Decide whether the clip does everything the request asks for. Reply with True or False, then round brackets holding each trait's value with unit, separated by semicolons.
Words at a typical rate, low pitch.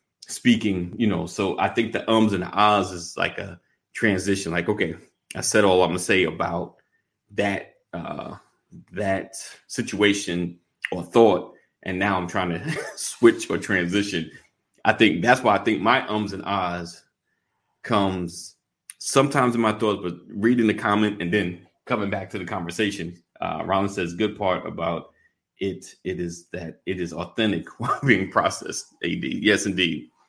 True (165 wpm; 95 Hz)